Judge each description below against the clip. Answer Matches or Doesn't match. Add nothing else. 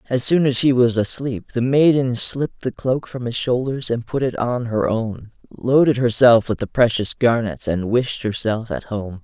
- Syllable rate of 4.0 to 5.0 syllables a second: Matches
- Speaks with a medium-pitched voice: Doesn't match